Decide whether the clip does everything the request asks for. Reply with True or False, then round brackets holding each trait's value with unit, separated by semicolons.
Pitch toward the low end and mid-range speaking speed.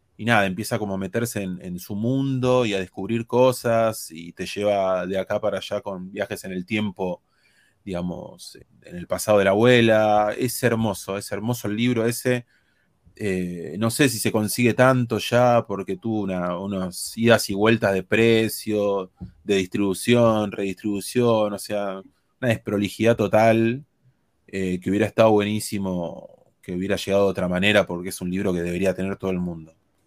True (105 Hz; 170 wpm)